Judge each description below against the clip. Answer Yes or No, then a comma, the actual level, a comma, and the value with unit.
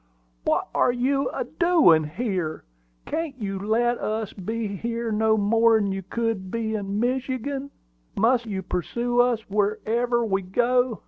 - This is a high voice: Yes, high, 225 Hz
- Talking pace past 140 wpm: No, slow, 135 wpm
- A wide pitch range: No, average, 3.3 semitones